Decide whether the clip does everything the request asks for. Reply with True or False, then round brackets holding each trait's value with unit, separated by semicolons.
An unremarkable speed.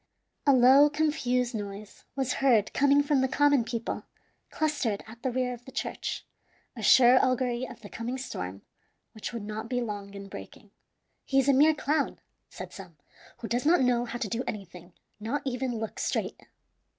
True (180 wpm)